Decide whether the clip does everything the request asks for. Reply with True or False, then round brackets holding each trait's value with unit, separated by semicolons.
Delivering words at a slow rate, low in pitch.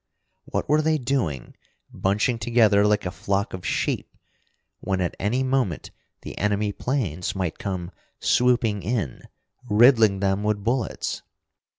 True (130 wpm; 105 Hz)